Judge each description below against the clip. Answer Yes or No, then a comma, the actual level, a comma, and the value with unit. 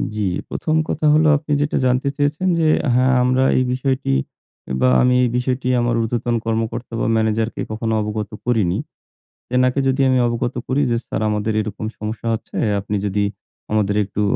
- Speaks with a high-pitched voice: No, low, 120 Hz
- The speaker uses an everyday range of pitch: Yes, average, 3.1 semitones